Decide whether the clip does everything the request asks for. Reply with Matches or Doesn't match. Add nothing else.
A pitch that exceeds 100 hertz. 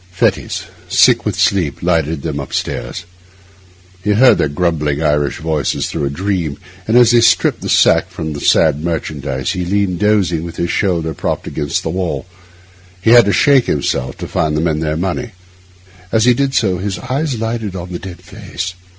Doesn't match